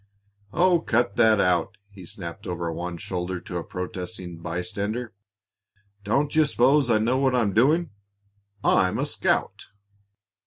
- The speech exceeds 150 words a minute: No, average, 140 wpm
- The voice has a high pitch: No, low, 105 Hz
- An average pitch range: No, wide, 5.7 semitones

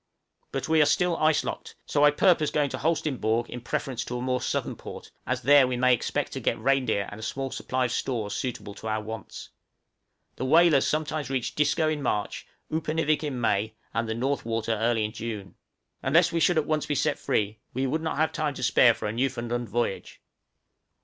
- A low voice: Yes, low, 130 Hz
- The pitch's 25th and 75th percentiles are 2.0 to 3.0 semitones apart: No, average, 4.8 semitones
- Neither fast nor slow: No, fast, 210 wpm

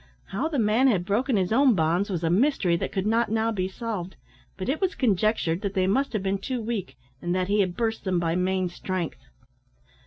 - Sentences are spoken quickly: Yes, fast, 215 wpm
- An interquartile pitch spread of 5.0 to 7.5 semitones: No, average, 3.9 semitones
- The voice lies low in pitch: No, high, 200 Hz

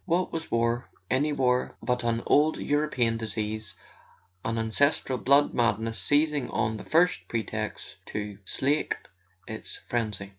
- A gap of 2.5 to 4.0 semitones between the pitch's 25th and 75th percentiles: No, average, 4.6 semitones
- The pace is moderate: No, slow, 120 wpm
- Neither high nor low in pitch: No, low, 120 Hz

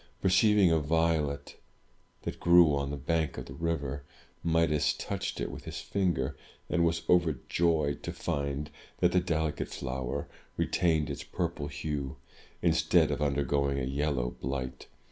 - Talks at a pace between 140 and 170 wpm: Yes, average, 145 wpm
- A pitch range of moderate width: Yes, average, 3.0 semitones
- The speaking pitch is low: Yes, very low, 75 Hz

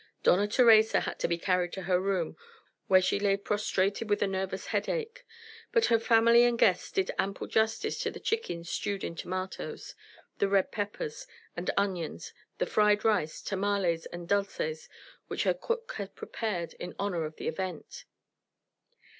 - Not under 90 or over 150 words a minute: No, average, 160 wpm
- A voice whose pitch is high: Yes, high, 200 Hz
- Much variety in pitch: No, average, 3.3 semitones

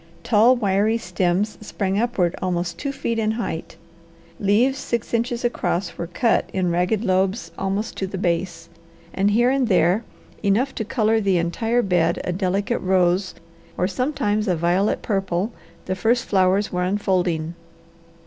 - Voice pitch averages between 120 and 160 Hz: No, high, 195 Hz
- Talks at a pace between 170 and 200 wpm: No, average, 150 wpm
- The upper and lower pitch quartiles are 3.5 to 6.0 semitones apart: Yes, average, 3.8 semitones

